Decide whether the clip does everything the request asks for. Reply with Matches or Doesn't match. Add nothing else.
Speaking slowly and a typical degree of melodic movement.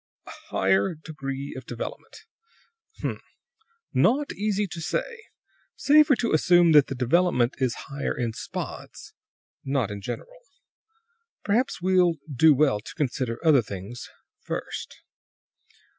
Doesn't match